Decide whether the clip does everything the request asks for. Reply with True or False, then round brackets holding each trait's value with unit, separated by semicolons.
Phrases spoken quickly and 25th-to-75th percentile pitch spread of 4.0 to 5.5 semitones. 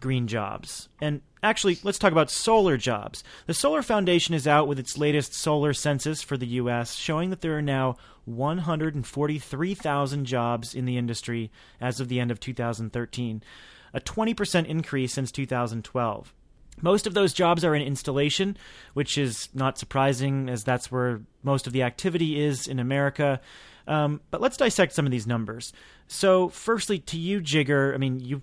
False (170 wpm; 4.7 semitones)